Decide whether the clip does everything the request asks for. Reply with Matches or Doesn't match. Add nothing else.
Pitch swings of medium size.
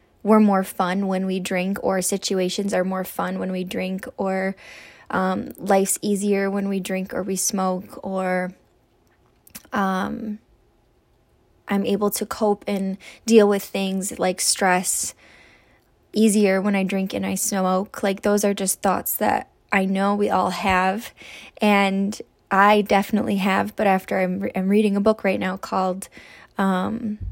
Doesn't match